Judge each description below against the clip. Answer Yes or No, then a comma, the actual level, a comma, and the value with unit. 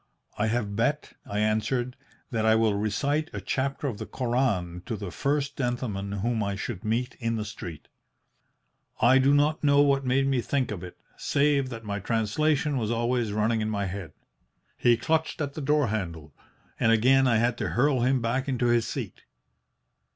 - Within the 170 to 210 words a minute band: Yes, average, 185 wpm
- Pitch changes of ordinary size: Yes, average, 4.2 semitones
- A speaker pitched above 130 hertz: No, low, 120 Hz